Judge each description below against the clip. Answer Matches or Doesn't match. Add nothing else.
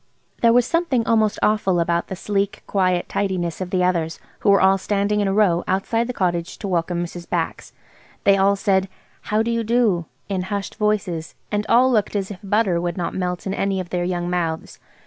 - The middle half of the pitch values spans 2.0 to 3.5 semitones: Matches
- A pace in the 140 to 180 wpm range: Doesn't match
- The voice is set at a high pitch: Matches